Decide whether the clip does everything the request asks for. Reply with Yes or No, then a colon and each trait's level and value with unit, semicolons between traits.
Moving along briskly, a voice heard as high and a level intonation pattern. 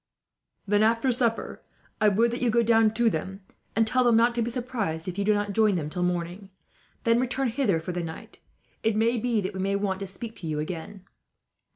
No: fast, 225 wpm; high, 215 Hz; average, 3.7 semitones